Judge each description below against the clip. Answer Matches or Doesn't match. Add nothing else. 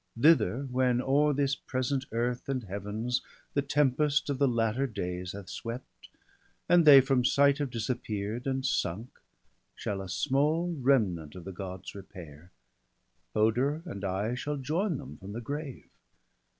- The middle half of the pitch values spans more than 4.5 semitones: Matches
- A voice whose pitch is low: Matches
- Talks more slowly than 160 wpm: Matches